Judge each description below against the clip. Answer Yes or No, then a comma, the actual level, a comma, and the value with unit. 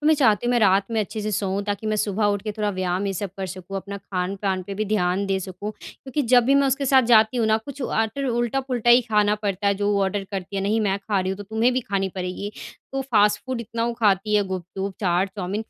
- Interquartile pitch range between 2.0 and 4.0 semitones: Yes, average, 2.9 semitones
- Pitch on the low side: No, high, 205 Hz